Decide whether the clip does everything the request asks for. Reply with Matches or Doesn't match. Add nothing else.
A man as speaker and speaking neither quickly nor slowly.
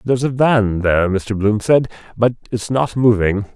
Matches